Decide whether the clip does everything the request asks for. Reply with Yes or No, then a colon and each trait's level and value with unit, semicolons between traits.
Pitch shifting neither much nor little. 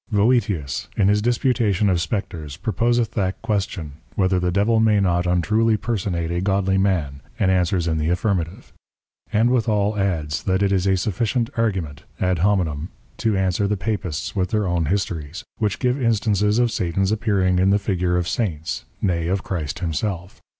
Yes: average, 3.4 semitones